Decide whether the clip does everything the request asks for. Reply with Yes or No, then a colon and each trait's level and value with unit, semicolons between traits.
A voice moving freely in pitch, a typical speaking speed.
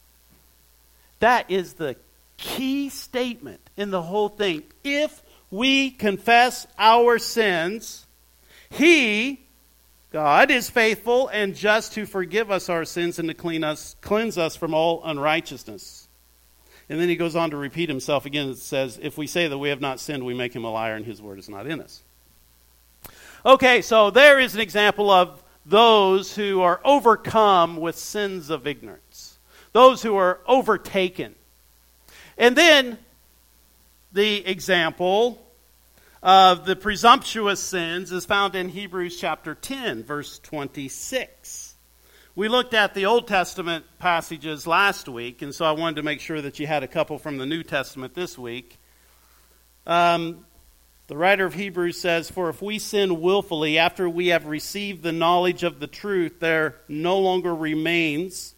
Yes: wide, 6.9 semitones; average, 155 wpm